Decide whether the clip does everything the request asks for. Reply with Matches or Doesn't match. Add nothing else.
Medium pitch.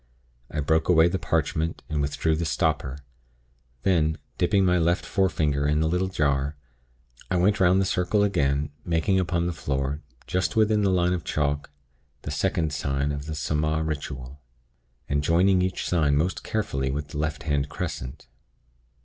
Doesn't match